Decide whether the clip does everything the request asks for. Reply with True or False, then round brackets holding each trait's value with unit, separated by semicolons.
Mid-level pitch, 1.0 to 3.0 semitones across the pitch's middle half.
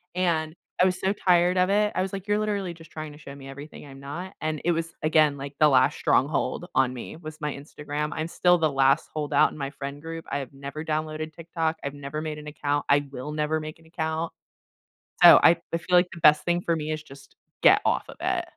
True (155 Hz; 2.6 semitones)